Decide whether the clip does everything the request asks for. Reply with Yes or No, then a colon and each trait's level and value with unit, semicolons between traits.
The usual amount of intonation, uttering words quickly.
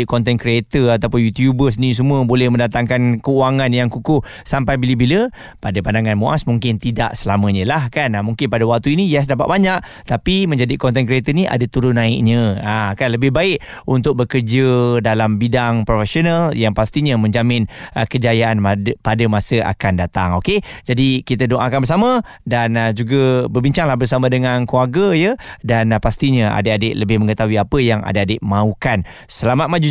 Yes: average, 3.0 semitones; fast, 160 wpm